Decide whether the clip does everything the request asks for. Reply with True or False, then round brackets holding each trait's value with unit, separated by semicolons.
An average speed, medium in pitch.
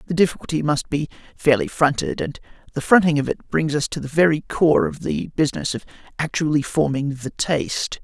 True (185 wpm; 145 Hz)